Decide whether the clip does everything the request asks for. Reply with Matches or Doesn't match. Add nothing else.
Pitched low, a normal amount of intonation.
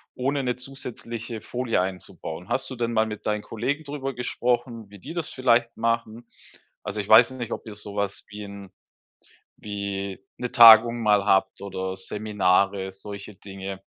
Matches